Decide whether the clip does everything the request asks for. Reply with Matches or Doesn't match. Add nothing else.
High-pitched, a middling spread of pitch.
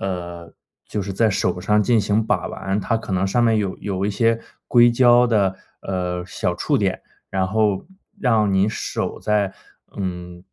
Doesn't match